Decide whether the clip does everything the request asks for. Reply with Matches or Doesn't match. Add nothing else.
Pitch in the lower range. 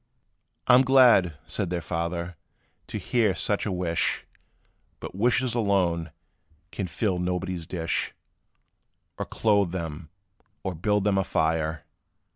Matches